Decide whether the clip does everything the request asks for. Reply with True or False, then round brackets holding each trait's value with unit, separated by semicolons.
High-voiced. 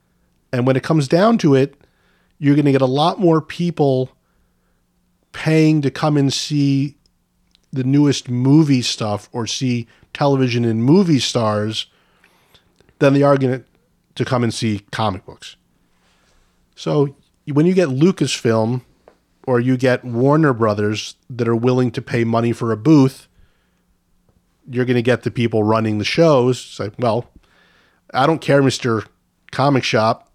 False (130 Hz)